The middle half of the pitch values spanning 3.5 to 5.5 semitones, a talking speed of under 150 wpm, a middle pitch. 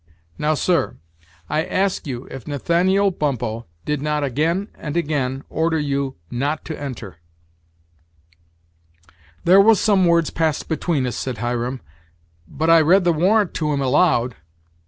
Yes: average, 4.3 semitones; average, 140 wpm; medium, 150 Hz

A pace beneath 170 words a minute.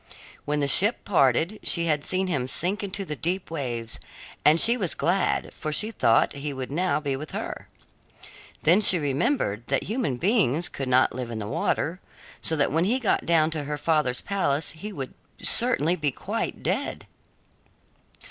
No: average, 175 wpm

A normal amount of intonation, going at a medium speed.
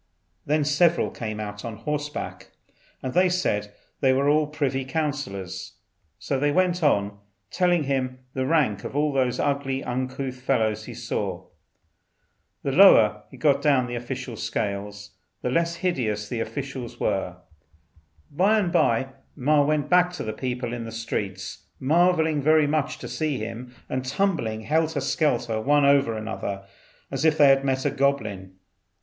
Yes: average, 4.8 semitones; average, 155 wpm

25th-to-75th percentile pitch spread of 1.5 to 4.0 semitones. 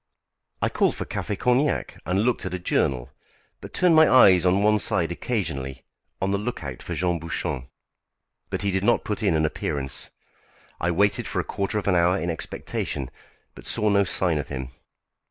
No: average, 4.7 semitones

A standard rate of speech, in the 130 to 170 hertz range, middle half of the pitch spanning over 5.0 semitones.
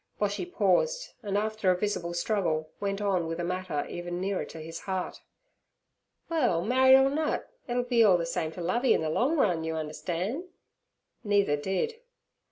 No: average, 170 wpm; high, 190 Hz; wide, 5.6 semitones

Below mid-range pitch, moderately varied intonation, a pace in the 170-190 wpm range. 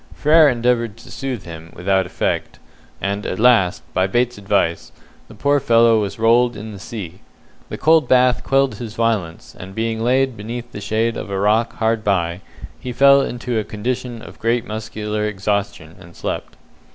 Yes: low, 110 Hz; average, 3.5 semitones; average, 175 wpm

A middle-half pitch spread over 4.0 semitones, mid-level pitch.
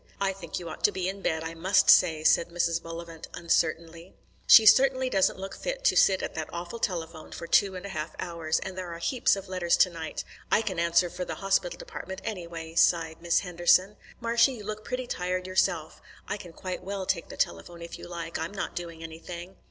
No: narrow, 2.5 semitones; medium, 175 Hz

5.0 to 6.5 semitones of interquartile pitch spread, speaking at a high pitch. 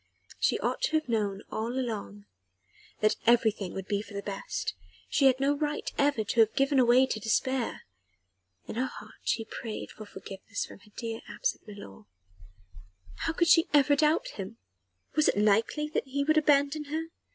Yes: average, 5.3 semitones; high, 240 Hz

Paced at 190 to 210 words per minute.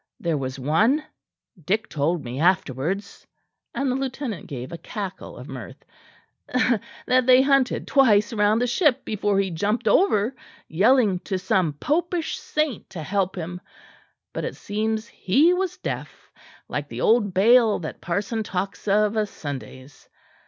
No: average, 145 wpm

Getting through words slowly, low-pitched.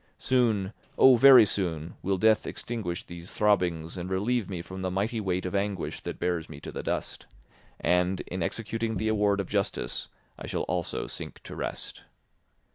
No: average, 175 wpm; very low, 95 Hz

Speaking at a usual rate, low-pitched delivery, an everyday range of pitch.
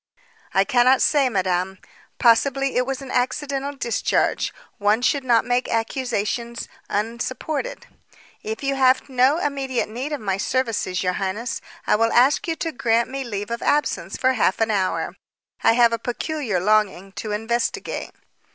No: average, 155 wpm; high, 240 Hz; average, 4.0 semitones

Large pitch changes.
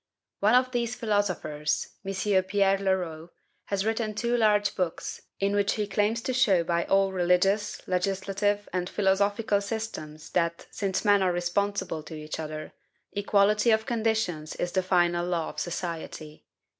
No: average, 3.0 semitones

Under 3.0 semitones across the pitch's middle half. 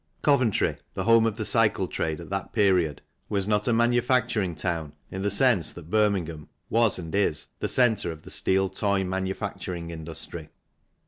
No: average, 4.4 semitones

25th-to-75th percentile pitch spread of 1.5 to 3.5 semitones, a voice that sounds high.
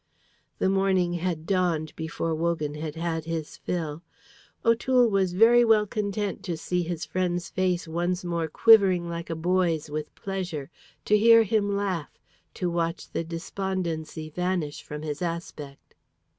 No: average, 3.0 semitones; medium, 175 Hz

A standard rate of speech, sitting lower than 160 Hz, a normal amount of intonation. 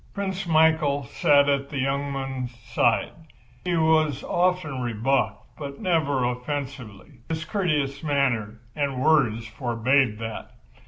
No: slow, 120 wpm; medium, 140 Hz; average, 4.2 semitones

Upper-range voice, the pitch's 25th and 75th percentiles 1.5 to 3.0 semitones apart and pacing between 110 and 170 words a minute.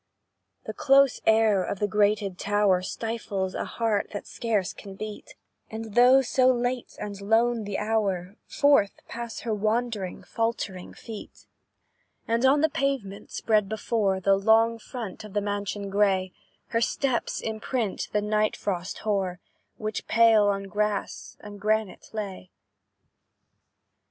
Yes: high, 210 Hz; narrow, 2.4 semitones; slow, 135 wpm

